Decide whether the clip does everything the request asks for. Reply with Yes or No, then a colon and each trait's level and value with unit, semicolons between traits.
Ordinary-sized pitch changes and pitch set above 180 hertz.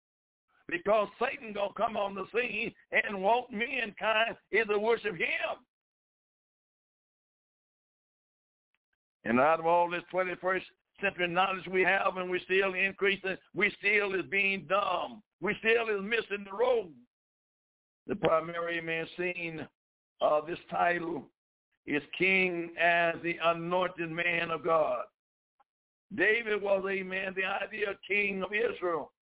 Yes: average, 3.1 semitones; high, 190 Hz